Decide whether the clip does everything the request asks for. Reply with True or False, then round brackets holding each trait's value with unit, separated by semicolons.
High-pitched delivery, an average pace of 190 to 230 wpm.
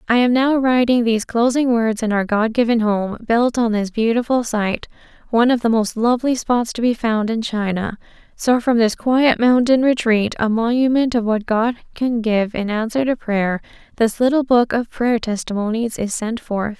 True (230 Hz; 195 wpm)